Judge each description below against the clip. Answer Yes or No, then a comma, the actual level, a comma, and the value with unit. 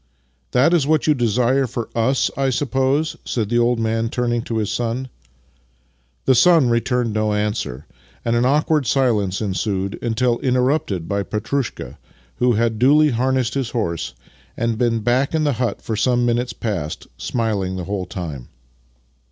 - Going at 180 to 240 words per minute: No, average, 165 wpm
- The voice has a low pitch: Yes, low, 120 Hz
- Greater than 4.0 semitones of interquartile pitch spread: No, average, 3.5 semitones